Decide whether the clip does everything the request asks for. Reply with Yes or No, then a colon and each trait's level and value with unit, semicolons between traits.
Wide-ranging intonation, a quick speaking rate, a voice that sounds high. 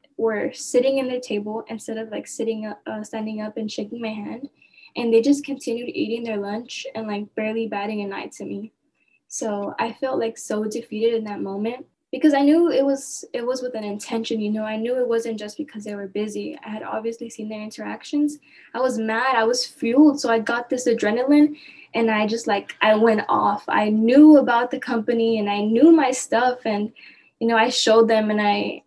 No: average, 3.2 semitones; fast, 215 wpm; high, 230 Hz